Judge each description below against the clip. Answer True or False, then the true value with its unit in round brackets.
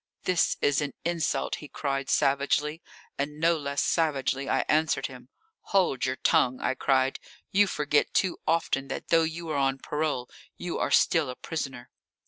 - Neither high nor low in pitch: True (145 Hz)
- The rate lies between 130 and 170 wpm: True (165 wpm)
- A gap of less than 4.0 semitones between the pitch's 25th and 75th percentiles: True (3.2 semitones)